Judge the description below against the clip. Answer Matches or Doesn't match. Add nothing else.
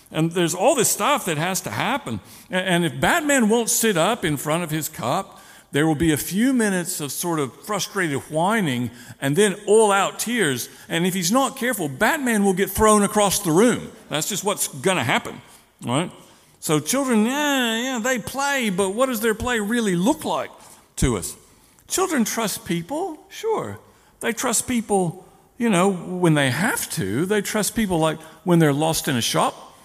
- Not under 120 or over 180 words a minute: Doesn't match